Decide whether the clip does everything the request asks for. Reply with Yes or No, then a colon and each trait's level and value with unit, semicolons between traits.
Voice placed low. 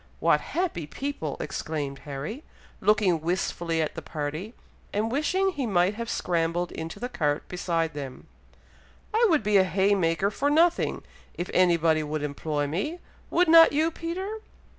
No: medium, 185 Hz